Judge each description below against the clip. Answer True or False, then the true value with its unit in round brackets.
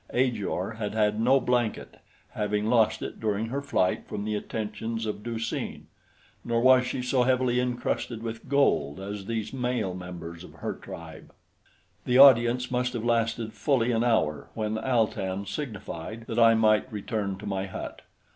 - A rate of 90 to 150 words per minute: False (165 wpm)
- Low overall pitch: True (115 Hz)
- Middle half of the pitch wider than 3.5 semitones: False (3.0 semitones)